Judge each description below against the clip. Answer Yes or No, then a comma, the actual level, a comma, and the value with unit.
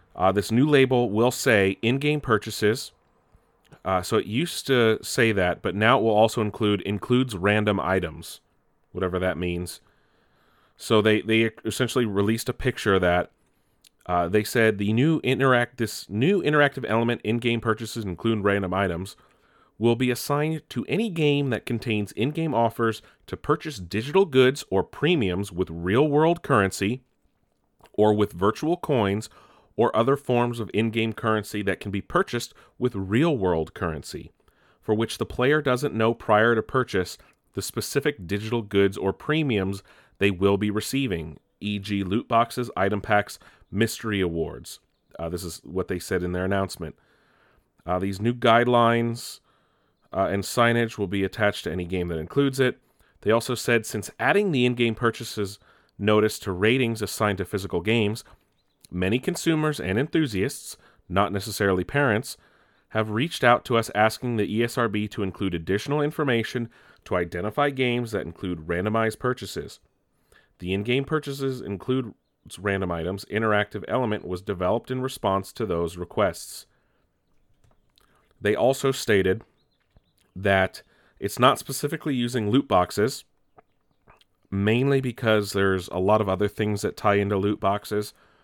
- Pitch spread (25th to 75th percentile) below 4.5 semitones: Yes, average, 4.0 semitones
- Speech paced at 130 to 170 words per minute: Yes, average, 150 wpm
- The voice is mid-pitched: No, low, 110 Hz